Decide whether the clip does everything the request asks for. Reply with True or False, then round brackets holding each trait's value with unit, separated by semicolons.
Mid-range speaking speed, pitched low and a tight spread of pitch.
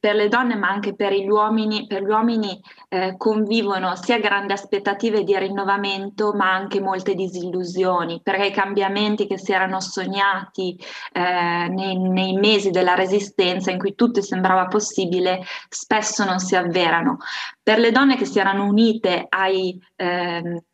False (155 wpm; 195 Hz; 2.0 semitones)